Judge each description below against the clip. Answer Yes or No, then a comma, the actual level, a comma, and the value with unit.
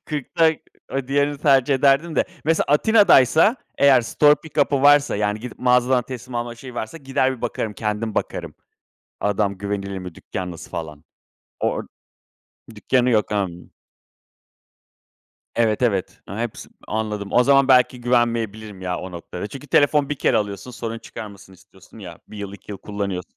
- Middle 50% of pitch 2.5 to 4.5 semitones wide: No, average, 5.1 semitones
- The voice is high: No, low, 115 Hz